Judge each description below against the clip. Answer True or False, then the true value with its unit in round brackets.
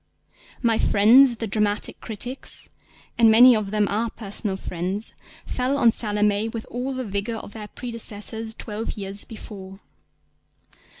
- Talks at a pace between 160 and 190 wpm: False (135 wpm)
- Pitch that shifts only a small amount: True (2.3 semitones)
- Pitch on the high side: True (220 Hz)